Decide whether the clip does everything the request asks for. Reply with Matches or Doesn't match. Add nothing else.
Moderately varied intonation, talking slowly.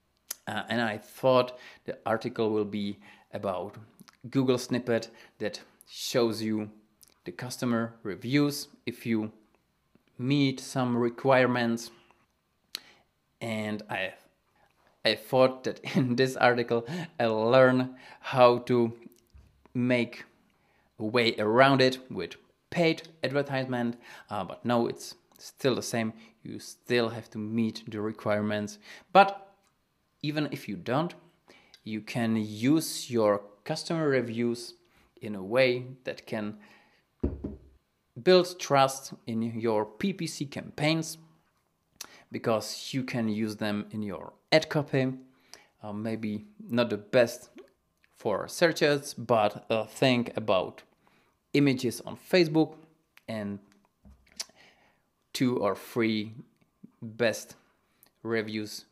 Matches